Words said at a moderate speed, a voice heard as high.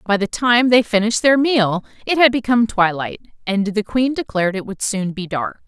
No: fast, 210 wpm; high, 220 Hz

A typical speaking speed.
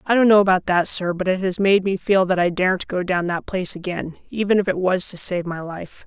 No: fast, 275 wpm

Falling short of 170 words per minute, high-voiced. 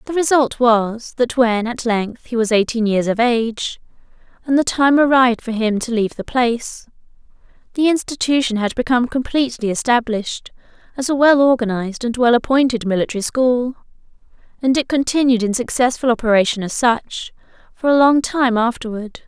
Yes: average, 160 wpm; high, 240 Hz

